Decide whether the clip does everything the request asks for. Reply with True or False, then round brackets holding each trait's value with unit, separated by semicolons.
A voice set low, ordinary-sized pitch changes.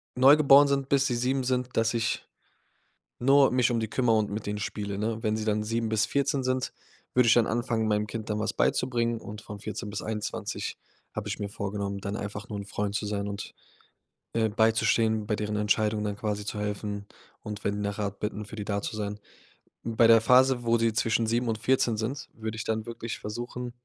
False (110 Hz; 2.2 semitones)